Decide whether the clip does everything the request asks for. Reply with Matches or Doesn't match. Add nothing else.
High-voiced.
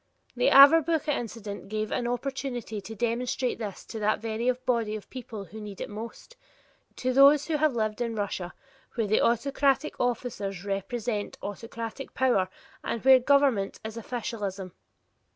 Matches